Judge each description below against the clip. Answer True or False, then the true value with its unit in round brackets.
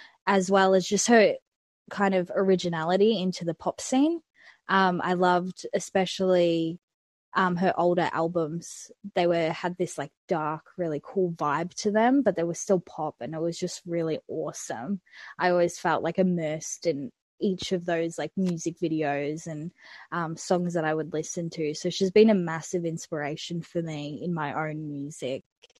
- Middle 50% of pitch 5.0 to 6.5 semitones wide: False (2.7 semitones)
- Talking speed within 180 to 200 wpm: False (170 wpm)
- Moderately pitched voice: True (175 Hz)